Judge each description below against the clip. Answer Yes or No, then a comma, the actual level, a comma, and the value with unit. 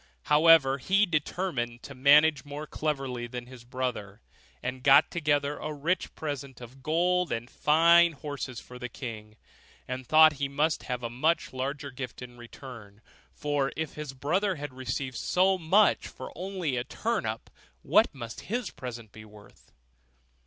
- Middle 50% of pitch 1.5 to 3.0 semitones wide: No, average, 4.0 semitones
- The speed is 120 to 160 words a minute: Yes, average, 155 wpm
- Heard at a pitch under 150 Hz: Yes, medium, 140 Hz